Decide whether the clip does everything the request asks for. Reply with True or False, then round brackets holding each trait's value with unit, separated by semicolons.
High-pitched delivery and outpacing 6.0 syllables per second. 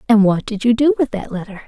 True (225 Hz; 6.3 syllables/s)